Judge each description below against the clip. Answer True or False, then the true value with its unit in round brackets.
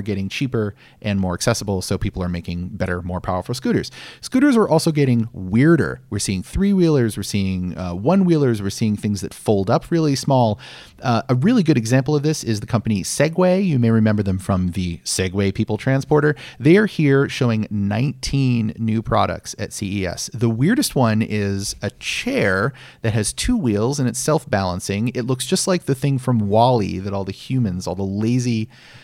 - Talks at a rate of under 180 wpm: False (190 wpm)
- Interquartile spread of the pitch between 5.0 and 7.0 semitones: True (5.5 semitones)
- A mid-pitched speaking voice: False (115 Hz)